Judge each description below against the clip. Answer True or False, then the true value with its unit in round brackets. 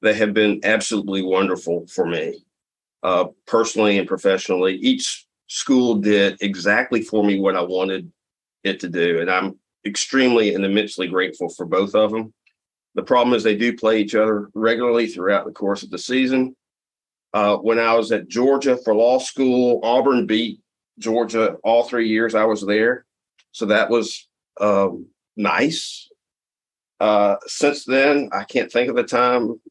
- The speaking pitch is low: True (110 Hz)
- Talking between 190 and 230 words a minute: False (160 wpm)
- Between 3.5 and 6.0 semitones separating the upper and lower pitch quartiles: False (3.0 semitones)